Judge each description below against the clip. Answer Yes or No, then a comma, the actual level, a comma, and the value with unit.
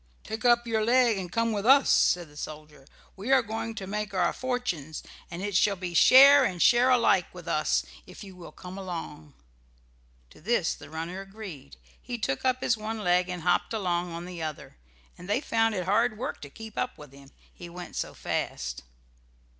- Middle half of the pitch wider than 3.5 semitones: Yes, average, 4.9 semitones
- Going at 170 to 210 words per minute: Yes, average, 200 wpm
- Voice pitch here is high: Yes, high, 195 Hz